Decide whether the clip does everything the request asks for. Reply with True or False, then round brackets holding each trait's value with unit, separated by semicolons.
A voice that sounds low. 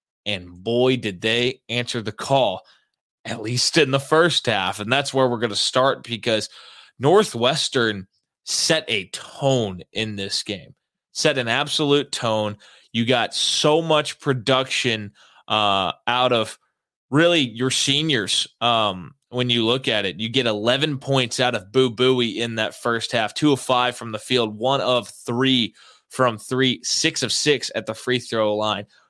True (125 Hz)